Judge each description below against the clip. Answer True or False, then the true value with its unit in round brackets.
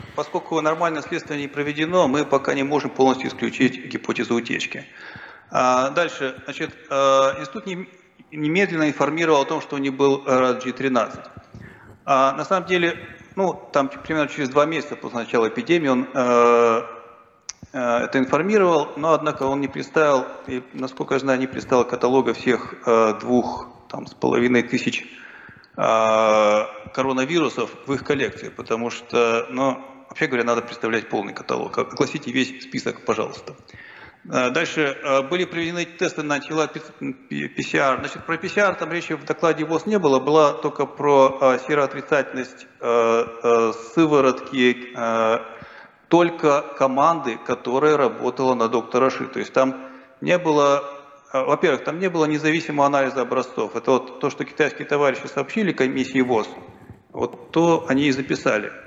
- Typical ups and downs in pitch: True (3.5 semitones)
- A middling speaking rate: True (135 wpm)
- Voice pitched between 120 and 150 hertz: True (140 Hz)